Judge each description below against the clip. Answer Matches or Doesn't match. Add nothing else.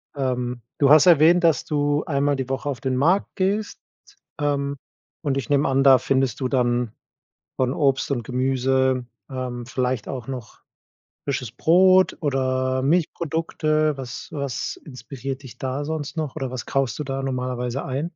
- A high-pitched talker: Doesn't match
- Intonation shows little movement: Matches